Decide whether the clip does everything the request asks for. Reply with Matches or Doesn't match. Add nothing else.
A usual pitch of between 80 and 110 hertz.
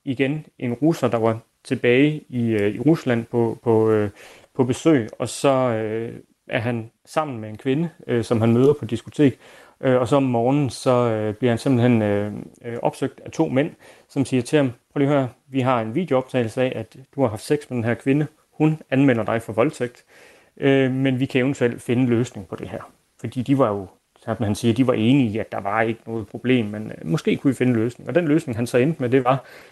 Doesn't match